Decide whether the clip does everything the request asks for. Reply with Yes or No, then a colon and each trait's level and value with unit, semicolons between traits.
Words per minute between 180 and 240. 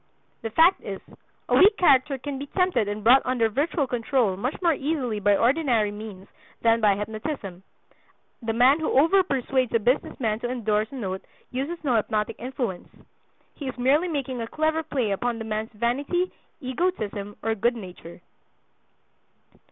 No: average, 160 wpm